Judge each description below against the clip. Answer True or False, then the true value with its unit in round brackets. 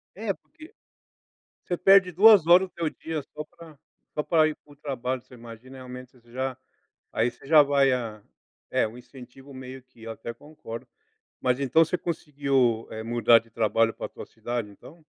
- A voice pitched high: False (130 Hz)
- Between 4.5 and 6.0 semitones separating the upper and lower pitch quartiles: True (4.8 semitones)